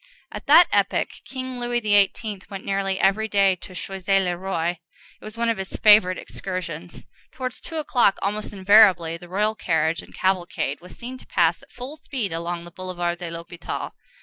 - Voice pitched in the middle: No, high, 195 Hz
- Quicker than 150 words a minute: Yes, average, 180 wpm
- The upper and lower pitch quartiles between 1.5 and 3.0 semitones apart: No, average, 3.7 semitones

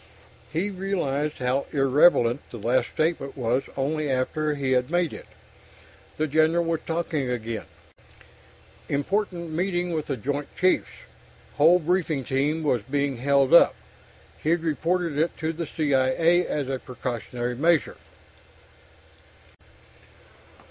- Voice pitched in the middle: Yes, medium, 150 Hz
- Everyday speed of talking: No, slow, 120 wpm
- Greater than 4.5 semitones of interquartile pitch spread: No, average, 4.1 semitones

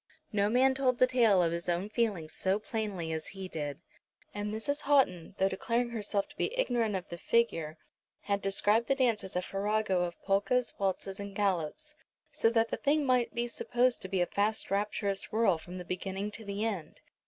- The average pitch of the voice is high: Yes, high, 205 Hz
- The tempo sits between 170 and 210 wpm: Yes, average, 200 wpm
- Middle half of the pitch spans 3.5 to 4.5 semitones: Yes, average, 3.9 semitones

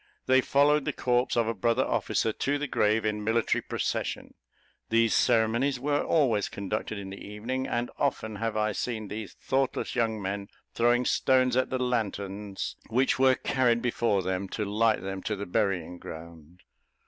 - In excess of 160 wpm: Yes, average, 170 wpm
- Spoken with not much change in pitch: No, average, 3.8 semitones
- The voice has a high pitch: No, low, 115 Hz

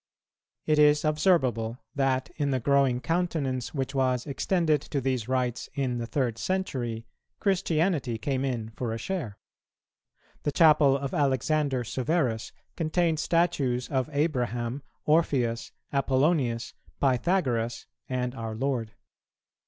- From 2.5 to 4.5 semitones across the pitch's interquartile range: Yes, average, 3.9 semitones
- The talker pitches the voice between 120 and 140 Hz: Yes, low, 135 Hz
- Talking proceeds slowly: Yes, slow, 120 wpm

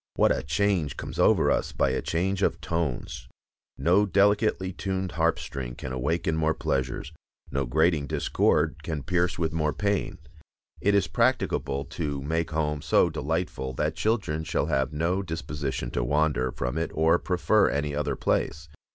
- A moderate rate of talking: Yes, average, 160 wpm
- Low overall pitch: Yes, very low, 80 Hz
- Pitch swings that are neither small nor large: Yes, average, 3.7 semitones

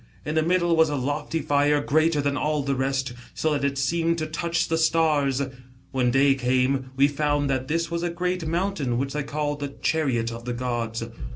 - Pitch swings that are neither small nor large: Yes, average, 3.1 semitones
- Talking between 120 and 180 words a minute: No, fast, 205 wpm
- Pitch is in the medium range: Yes, medium, 145 Hz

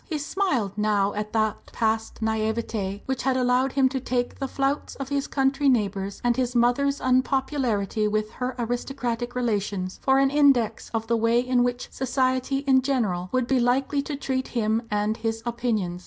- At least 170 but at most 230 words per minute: Yes, average, 175 wpm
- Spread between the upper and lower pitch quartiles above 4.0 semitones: No, average, 3.5 semitones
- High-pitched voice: Yes, high, 245 Hz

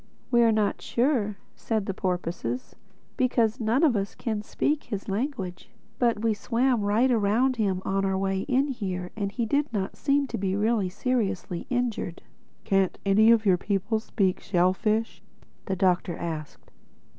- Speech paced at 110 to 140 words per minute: No, average, 155 wpm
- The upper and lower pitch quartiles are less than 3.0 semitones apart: No, average, 3.7 semitones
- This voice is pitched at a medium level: No, high, 210 Hz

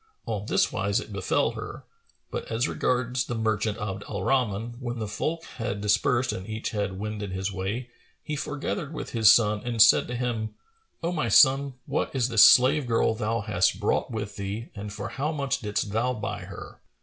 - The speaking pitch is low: Yes, low, 110 Hz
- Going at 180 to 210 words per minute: Yes, average, 195 wpm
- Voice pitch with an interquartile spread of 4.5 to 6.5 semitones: No, average, 3.5 semitones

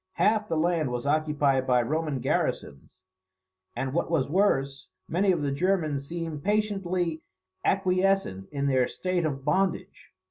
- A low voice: No, medium, 155 Hz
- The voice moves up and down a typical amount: Yes, average, 5.0 semitones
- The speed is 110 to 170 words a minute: Yes, average, 140 wpm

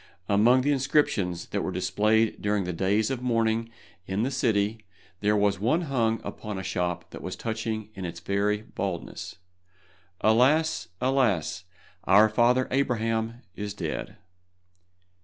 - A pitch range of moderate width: Yes, average, 3.5 semitones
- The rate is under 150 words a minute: Yes, average, 140 wpm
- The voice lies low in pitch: Yes, low, 110 Hz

